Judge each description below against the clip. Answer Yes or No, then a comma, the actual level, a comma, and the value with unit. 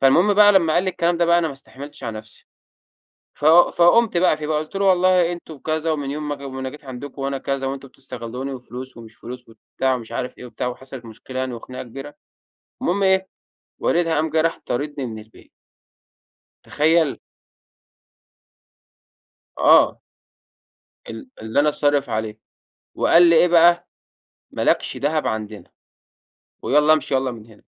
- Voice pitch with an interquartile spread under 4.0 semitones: No, average, 4.7 semitones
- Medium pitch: Yes, medium, 145 Hz